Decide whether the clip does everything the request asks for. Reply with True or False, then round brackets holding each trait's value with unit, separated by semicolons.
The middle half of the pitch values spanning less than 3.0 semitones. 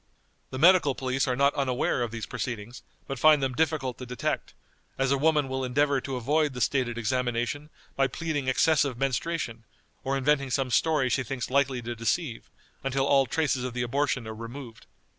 True (2.5 semitones)